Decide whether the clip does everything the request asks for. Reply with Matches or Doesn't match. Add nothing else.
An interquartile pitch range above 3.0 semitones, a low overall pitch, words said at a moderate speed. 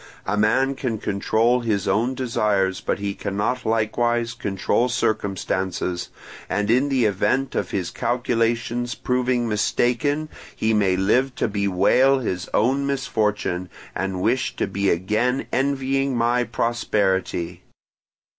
Doesn't match